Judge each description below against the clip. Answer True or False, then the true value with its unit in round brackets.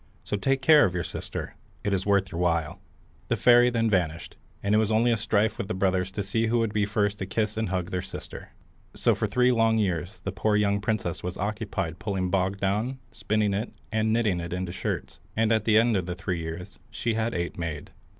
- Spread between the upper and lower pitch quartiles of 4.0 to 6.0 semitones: False (3.2 semitones)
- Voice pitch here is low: True (100 Hz)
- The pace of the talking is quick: True (225 wpm)